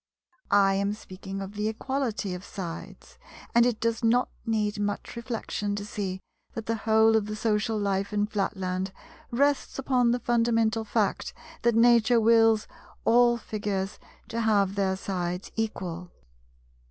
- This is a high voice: Yes, high, 215 Hz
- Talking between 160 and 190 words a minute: No, average, 145 wpm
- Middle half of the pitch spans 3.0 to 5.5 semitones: No, narrow, 2.6 semitones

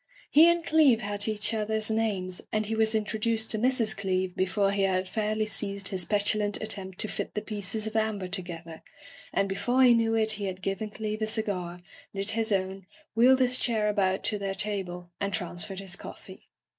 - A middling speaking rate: Yes, average, 195 wpm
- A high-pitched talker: Yes, high, 210 Hz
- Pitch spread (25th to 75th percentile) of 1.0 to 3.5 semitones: Yes, narrow, 2.4 semitones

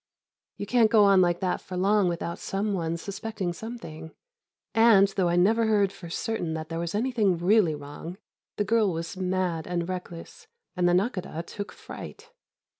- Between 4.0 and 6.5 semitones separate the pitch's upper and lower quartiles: No, average, 3.6 semitones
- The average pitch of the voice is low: No, medium, 185 Hz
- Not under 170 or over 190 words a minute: Yes, average, 175 wpm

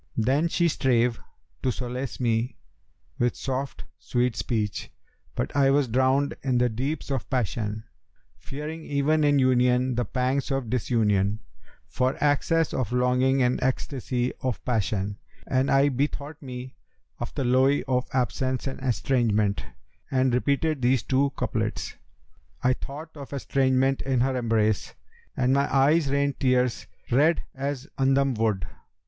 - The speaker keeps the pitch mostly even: Yes, narrow, 2.1 semitones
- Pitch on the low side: Yes, low, 130 Hz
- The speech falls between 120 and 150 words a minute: Yes, average, 140 wpm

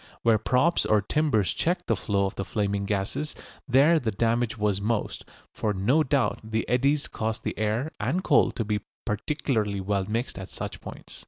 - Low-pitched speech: Yes, low, 110 Hz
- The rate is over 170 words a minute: Yes, average, 180 wpm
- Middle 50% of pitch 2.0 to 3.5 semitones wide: No, average, 4.7 semitones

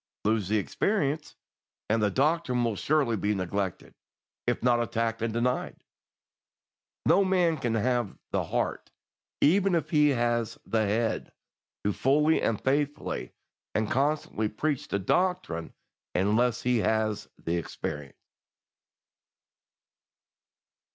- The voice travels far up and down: Yes, wide, 5.7 semitones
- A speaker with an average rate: No, slow, 115 wpm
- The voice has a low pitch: Yes, low, 120 Hz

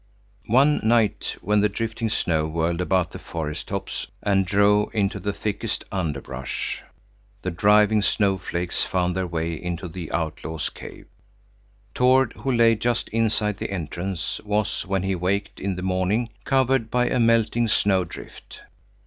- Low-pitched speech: Yes, low, 100 Hz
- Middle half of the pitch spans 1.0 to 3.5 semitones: No, average, 3.9 semitones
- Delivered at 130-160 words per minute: Yes, average, 145 wpm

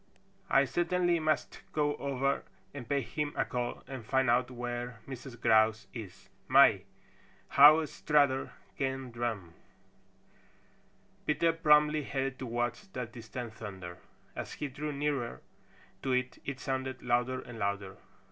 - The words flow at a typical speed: No, slow, 130 wpm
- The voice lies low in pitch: Yes, low, 130 Hz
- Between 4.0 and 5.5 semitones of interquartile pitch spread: No, average, 3.2 semitones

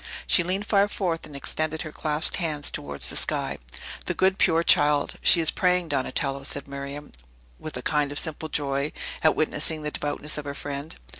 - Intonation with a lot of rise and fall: No, narrow, 2.4 semitones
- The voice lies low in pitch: No, medium, 150 Hz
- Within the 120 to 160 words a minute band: No, average, 190 wpm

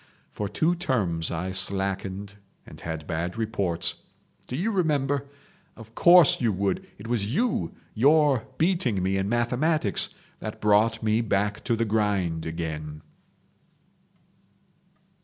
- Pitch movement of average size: No, wide, 5.8 semitones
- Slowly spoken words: Yes, slow, 120 wpm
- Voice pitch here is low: Yes, low, 105 Hz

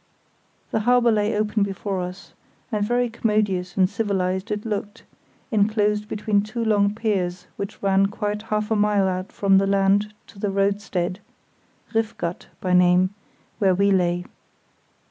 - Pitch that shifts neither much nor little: No, narrow, 1.9 semitones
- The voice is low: No, high, 205 Hz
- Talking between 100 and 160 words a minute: Yes, average, 150 wpm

